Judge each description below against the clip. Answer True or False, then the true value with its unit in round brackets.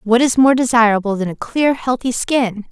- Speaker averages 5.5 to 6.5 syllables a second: False (4.9 syllables/s)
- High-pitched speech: True (235 Hz)